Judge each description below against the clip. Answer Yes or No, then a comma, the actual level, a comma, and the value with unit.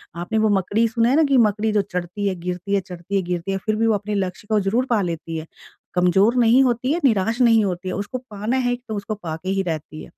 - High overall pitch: Yes, high, 205 Hz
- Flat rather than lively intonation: No, average, 3.9 semitones